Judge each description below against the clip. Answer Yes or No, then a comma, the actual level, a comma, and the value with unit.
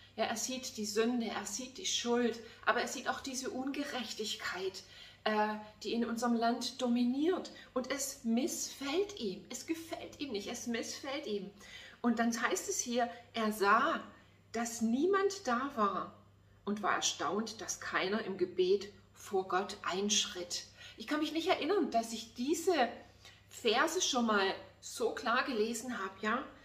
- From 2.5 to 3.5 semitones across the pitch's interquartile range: No, average, 4.9 semitones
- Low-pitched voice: No, high, 240 Hz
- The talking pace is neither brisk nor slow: Yes, average, 155 wpm